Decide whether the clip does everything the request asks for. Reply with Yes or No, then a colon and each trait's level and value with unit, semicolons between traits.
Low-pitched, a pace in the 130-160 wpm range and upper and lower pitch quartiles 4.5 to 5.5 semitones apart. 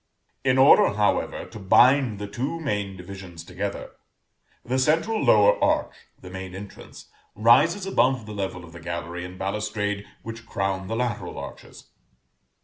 Yes: low, 105 Hz; average, 145 wpm; average, 4.8 semitones